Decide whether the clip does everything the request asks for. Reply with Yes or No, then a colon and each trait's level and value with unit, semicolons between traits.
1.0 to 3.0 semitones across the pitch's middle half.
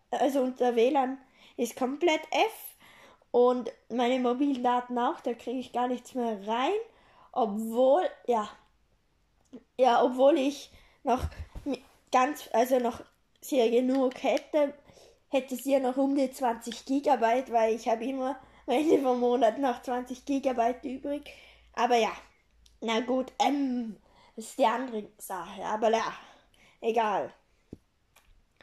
Yes: narrow, 2.5 semitones